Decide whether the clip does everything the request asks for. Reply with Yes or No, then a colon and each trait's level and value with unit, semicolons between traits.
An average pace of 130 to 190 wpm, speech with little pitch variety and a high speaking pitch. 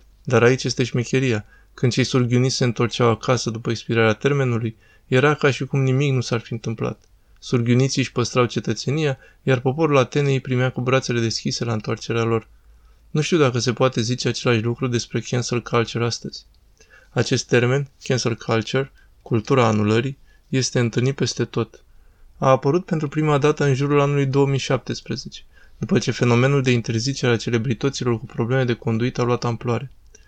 No: average, 165 wpm; narrow, 2.3 semitones; low, 125 Hz